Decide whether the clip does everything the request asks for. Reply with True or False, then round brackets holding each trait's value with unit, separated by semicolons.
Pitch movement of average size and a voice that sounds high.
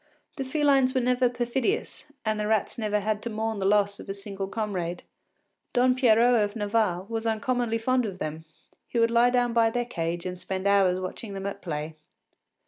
True (3.7 semitones; 220 Hz)